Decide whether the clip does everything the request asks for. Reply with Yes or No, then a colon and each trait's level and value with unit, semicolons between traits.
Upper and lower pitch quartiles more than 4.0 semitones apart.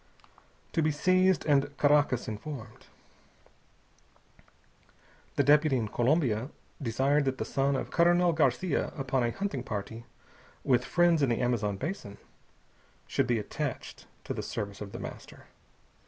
Yes: average, 4.6 semitones